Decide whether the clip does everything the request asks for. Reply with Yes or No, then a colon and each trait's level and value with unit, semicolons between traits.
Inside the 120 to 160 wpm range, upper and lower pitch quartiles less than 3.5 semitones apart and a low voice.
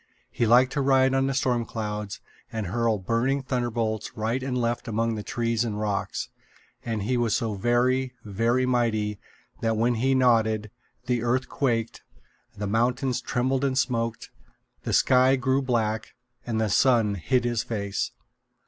Yes: average, 155 wpm; narrow, 2.6 semitones; low, 120 Hz